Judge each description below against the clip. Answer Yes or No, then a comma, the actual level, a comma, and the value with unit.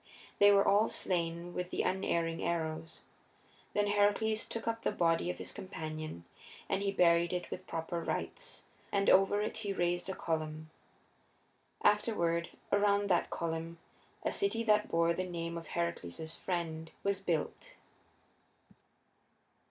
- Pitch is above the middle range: No, medium, 175 Hz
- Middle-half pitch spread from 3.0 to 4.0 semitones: Yes, average, 3.3 semitones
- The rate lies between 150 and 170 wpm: No, average, 140 wpm